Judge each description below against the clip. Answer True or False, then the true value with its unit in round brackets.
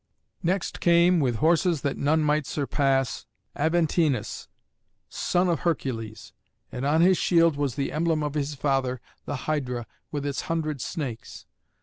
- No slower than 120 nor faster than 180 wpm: True (140 wpm)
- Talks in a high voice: False (150 Hz)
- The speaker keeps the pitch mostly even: False (3.6 semitones)